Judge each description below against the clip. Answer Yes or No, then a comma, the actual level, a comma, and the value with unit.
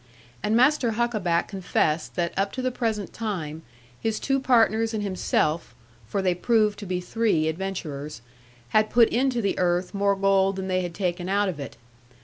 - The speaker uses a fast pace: No, average, 175 wpm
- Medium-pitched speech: No, high, 195 Hz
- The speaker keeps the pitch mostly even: No, average, 4.0 semitones